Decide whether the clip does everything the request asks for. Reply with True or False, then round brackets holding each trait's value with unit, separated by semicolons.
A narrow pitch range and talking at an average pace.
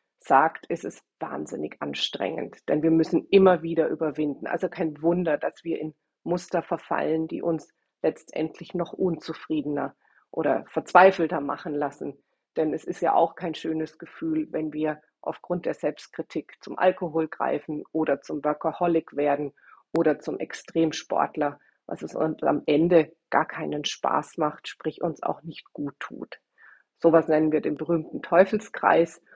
True (1.9 semitones; 150 wpm)